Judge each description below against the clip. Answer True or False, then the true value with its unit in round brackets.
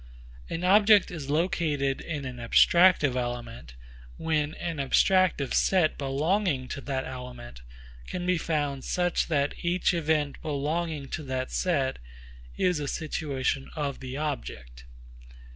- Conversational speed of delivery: False (125 wpm)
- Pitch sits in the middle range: True (145 Hz)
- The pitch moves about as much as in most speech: True (4.3 semitones)